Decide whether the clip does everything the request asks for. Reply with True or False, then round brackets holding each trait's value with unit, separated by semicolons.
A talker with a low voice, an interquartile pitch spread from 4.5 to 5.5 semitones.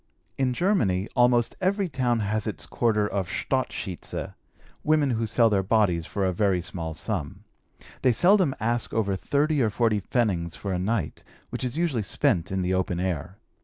True (110 Hz; 5.2 semitones)